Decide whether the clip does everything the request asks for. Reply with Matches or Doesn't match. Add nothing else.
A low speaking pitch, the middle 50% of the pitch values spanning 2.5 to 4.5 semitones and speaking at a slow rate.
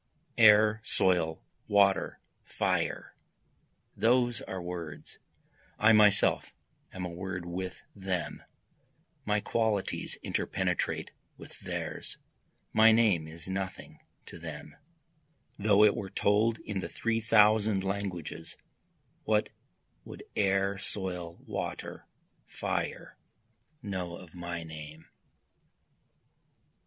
Matches